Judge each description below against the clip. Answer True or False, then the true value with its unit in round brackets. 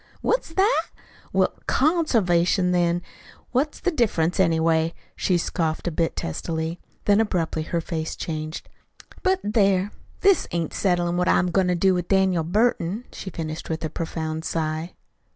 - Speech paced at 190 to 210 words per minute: False (150 wpm)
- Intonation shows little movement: False (3.6 semitones)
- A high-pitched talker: False (175 Hz)